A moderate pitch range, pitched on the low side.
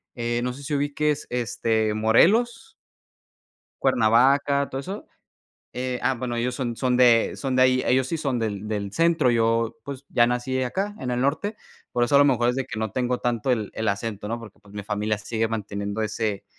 Yes: average, 3.4 semitones; low, 120 Hz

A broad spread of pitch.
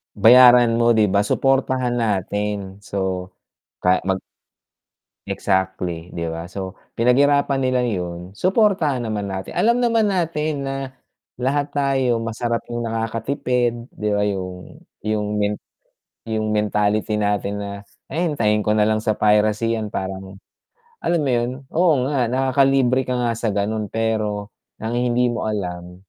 No: average, 3.9 semitones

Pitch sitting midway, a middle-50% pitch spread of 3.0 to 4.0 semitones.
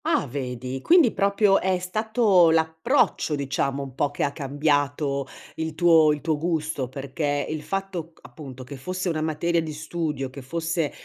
Yes: medium, 155 Hz; average, 3.7 semitones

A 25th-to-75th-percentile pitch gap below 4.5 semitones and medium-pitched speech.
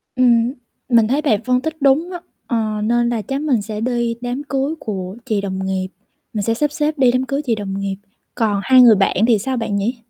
No: average, 4.0 semitones; high, 235 Hz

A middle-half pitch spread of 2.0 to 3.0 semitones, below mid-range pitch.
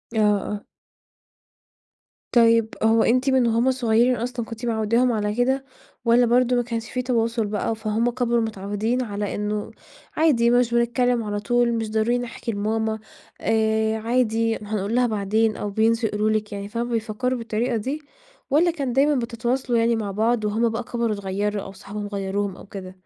No: narrow, 2.4 semitones; high, 225 Hz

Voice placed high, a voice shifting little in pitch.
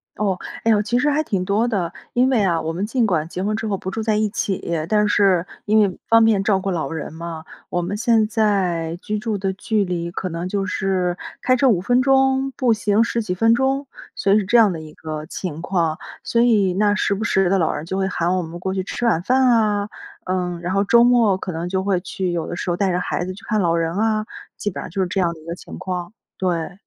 No: high, 195 Hz; average, 3.7 semitones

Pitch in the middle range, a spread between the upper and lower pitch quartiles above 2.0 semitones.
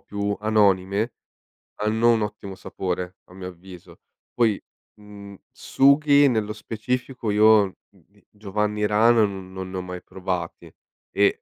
No: low, 105 Hz; narrow, 2.4 semitones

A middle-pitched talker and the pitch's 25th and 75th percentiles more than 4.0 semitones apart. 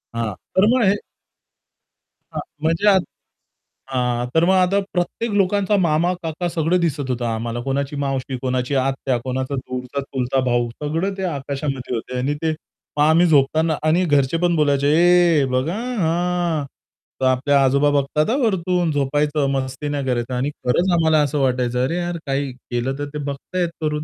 Yes: medium, 145 Hz; average, 4.4 semitones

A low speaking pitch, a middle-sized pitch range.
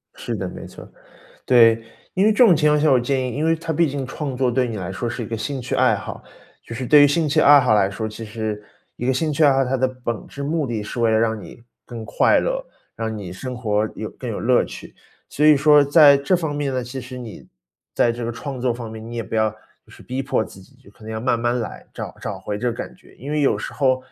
Yes: low, 125 Hz; average, 4.2 semitones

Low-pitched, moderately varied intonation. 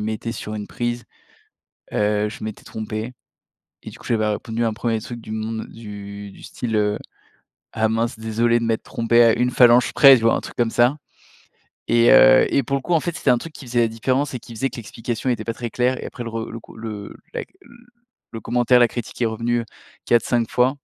No: low, 115 Hz; narrow, 1.7 semitones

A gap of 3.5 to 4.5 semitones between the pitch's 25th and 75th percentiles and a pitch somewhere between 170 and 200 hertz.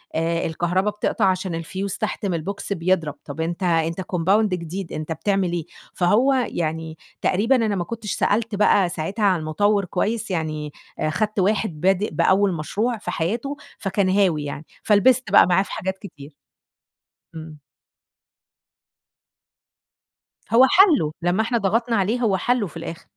Yes: average, 4.2 semitones; high, 190 Hz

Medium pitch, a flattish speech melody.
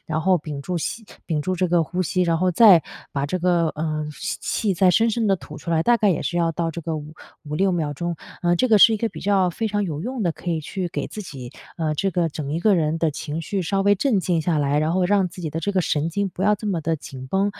No: medium, 175 Hz; average, 3.7 semitones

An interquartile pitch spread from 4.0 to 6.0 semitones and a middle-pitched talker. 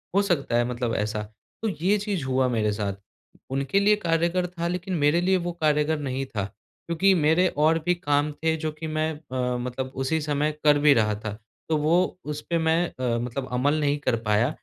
Yes: average, 4.6 semitones; medium, 150 Hz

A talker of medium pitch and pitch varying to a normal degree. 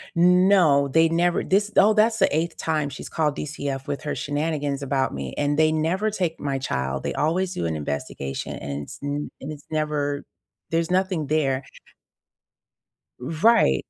Yes: medium, 150 Hz; average, 3.5 semitones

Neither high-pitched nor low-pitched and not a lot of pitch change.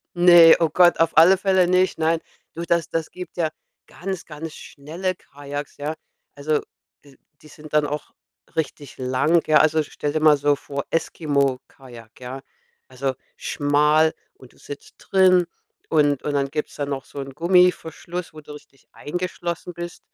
No: medium, 155 Hz; average, 3.1 semitones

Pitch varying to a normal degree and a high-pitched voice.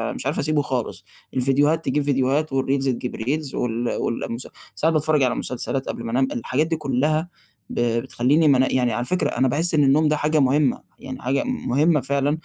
No: average, 3.1 semitones; low, 135 Hz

